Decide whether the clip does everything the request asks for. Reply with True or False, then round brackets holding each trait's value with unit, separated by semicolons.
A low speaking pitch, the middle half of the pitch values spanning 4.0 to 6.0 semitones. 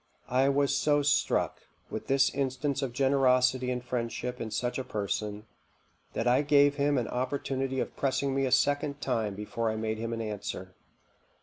False (130 Hz; 3.1 semitones)